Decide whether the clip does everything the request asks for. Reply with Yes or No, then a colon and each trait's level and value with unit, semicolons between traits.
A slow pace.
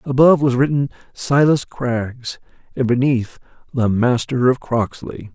Yes: slow, 125 wpm